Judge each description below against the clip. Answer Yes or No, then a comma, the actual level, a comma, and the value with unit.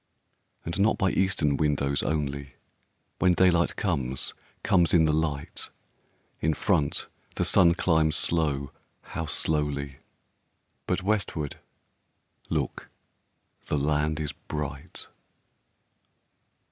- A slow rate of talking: Yes, slow, 90 wpm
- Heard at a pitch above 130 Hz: No, very low, 75 Hz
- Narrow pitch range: No, average, 3.0 semitones